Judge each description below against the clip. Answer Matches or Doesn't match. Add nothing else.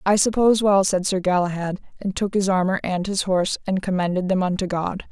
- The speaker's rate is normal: Doesn't match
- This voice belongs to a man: Doesn't match